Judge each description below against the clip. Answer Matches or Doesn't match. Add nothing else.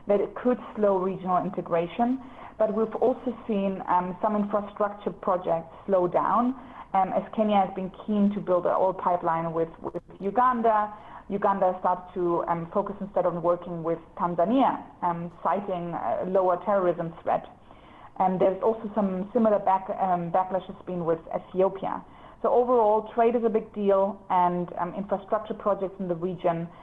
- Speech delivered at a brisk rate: Doesn't match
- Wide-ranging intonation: Doesn't match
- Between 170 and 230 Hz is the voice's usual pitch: Matches